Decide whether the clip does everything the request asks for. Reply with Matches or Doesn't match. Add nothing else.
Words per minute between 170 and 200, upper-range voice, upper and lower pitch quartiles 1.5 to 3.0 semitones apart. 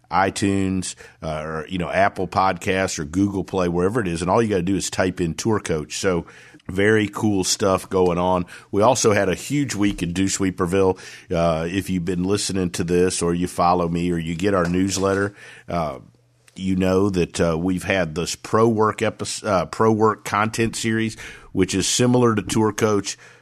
Doesn't match